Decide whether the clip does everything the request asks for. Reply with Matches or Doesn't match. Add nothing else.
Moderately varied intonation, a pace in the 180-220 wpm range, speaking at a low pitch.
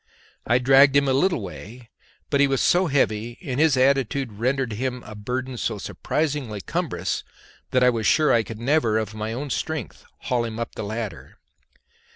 Matches